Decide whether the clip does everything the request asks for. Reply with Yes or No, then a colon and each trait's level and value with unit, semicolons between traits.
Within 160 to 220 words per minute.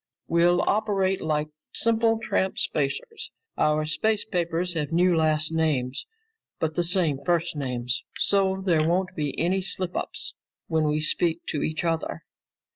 No: average, 145 wpm